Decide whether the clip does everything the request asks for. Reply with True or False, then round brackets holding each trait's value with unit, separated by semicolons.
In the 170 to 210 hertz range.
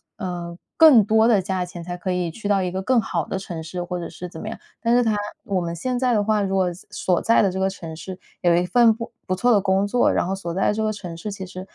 True (190 Hz)